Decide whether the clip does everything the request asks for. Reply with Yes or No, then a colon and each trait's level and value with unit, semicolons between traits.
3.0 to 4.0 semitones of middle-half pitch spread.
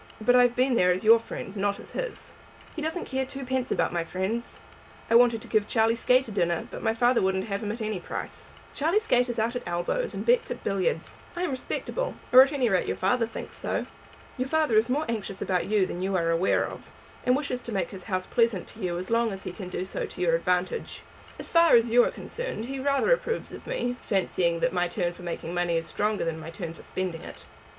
No: wide, 5.6 semitones